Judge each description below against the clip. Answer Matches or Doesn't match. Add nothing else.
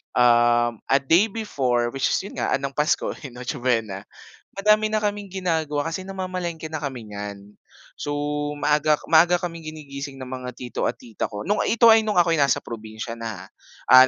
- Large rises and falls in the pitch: Matches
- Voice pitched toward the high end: Doesn't match